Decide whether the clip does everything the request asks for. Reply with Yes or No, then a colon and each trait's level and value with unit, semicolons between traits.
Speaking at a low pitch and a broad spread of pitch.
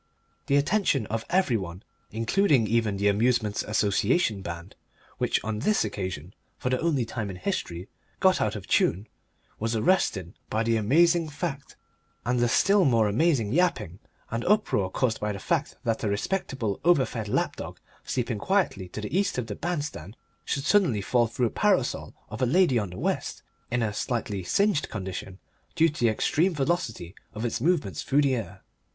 Yes: low, 115 Hz; wide, 7.0 semitones